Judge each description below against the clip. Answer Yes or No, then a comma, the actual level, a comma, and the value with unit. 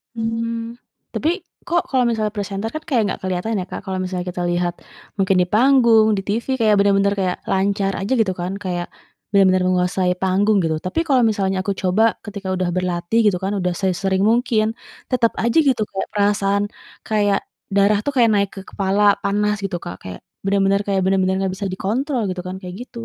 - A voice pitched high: Yes, high, 200 Hz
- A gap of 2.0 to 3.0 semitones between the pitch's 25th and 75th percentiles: Yes, average, 2.7 semitones